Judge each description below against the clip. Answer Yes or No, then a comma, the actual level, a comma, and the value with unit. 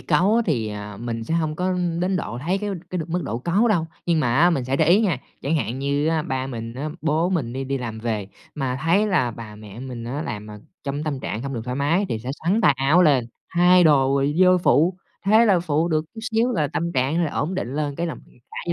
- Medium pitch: Yes, medium, 150 Hz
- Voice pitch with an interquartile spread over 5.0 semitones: Yes, wide, 5.6 semitones